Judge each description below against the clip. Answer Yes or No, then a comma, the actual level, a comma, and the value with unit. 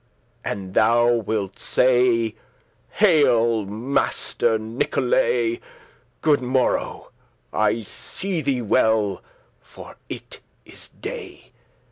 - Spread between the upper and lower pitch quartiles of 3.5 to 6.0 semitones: Yes, average, 3.9 semitones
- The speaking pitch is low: Yes, low, 120 Hz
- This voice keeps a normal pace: No, slow, 85 wpm